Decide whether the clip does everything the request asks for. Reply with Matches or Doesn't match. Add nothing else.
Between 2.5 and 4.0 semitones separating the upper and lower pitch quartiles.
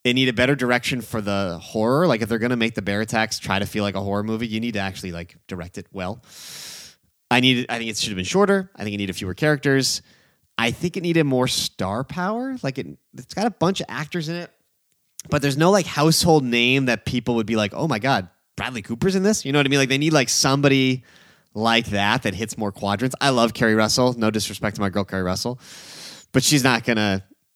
Doesn't match